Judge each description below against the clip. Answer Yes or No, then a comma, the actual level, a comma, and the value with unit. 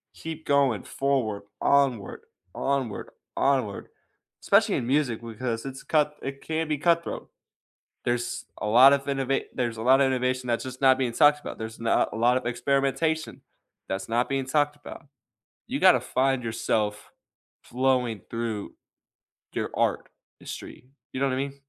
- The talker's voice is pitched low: Yes, low, 130 Hz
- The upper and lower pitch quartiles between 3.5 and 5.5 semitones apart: No, average, 3.0 semitones